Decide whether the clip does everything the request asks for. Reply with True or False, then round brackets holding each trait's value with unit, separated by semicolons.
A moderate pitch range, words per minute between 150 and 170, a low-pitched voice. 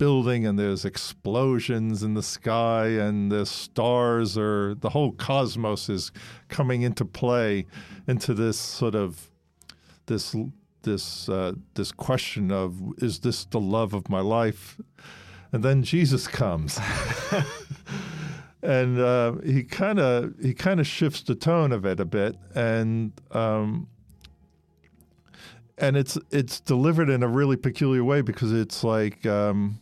False (4.4 semitones; 140 wpm; 115 Hz)